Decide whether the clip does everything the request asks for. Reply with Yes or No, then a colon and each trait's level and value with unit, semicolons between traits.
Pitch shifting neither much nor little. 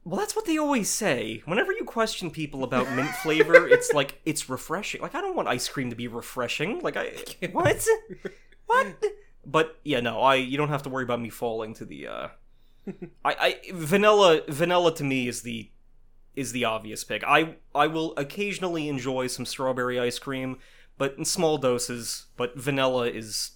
No: wide, 6.6 semitones